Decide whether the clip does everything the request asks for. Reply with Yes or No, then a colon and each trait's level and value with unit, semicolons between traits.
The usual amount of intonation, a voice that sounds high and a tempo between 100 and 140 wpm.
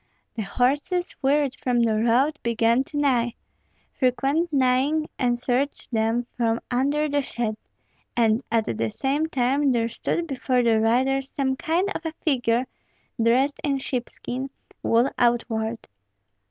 Yes: average, 3.3 semitones; very high, 255 Hz; slow, 135 wpm